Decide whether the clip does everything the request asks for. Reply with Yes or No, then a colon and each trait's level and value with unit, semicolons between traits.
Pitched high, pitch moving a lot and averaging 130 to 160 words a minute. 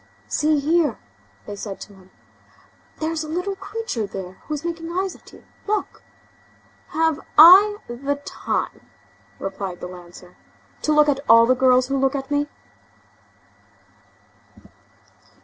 Yes: very high, 285 Hz; wide, 6.7 semitones; slow, 135 wpm